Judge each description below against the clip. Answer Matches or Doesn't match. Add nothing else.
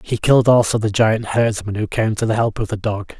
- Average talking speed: Doesn't match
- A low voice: Matches